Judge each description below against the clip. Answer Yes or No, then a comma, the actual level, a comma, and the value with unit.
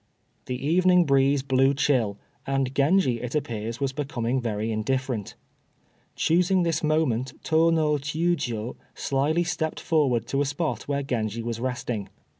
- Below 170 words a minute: Yes, average, 140 wpm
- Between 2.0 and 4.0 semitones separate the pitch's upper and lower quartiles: No, average, 4.5 semitones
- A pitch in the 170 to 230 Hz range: No, low, 135 Hz